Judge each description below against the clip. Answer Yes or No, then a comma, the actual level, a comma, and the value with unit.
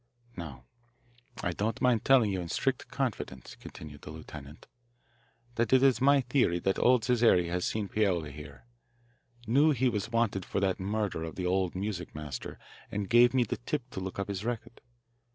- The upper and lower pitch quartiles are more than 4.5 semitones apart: Yes, wide, 5.5 semitones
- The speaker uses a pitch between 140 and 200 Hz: No, low, 100 Hz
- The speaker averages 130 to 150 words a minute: No, average, 175 wpm